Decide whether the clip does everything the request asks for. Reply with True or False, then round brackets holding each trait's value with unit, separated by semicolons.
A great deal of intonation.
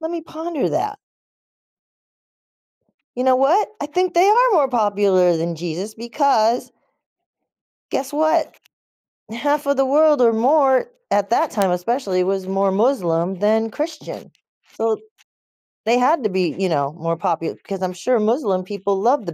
True (7.3 semitones)